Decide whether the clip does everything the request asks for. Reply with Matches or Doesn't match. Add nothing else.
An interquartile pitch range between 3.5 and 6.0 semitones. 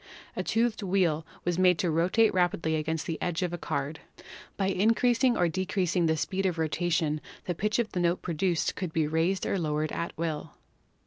Doesn't match